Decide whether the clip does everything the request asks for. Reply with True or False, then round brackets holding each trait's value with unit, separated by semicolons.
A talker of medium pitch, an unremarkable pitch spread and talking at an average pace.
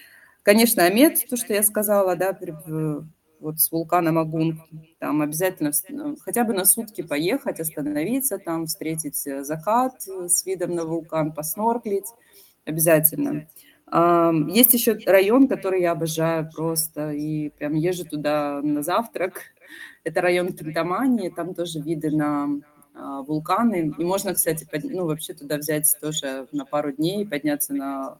True (165 Hz; 3.9 semitones; 135 wpm)